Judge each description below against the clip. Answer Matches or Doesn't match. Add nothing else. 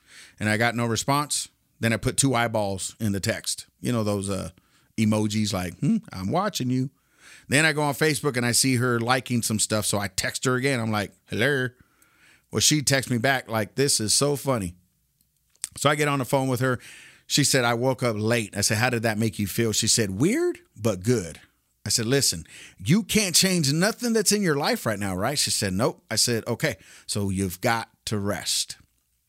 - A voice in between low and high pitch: Doesn't match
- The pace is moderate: Doesn't match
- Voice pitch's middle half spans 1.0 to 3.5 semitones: Doesn't match